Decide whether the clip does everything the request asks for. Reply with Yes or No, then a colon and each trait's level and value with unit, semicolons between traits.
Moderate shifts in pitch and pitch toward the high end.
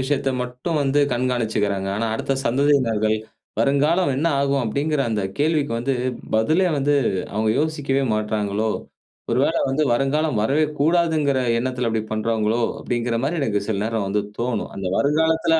No: average, 4.8 semitones; low, 130 Hz